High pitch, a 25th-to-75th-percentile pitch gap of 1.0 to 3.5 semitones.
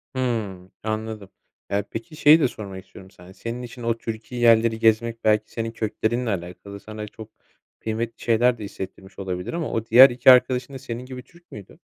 No: low, 115 Hz; average, 3.0 semitones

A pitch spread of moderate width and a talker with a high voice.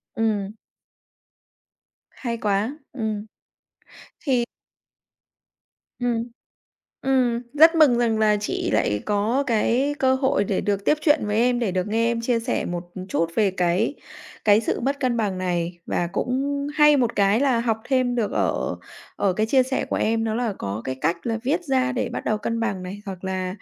Yes: average, 4.2 semitones; high, 225 Hz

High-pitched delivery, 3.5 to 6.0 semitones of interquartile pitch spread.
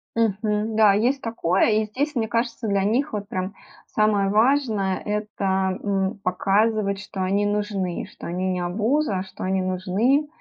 No: high, 205 Hz; average, 2.7 semitones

